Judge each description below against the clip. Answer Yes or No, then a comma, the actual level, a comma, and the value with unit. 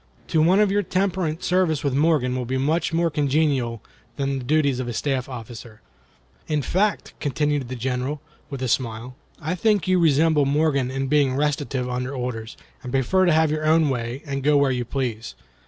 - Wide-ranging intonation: No, average, 3.8 semitones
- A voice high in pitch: No, medium, 140 Hz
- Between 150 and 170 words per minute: No, average, 190 wpm